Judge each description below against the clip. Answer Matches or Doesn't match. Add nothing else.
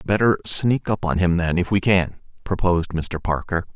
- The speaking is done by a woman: Doesn't match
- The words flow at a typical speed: Matches